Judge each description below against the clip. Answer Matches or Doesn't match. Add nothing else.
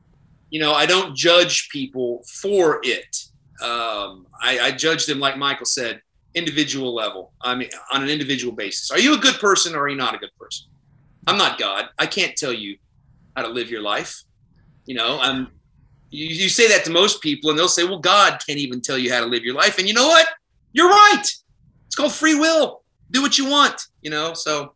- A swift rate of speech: Matches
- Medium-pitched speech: Matches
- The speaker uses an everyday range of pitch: Doesn't match